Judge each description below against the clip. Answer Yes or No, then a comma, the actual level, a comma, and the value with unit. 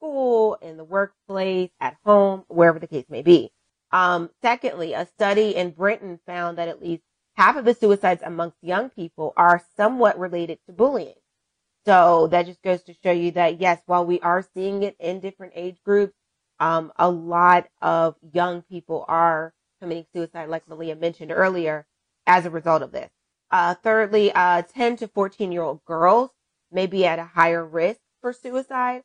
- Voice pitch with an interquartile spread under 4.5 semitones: Yes, average, 3.2 semitones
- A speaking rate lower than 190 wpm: Yes, average, 180 wpm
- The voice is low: No, medium, 180 Hz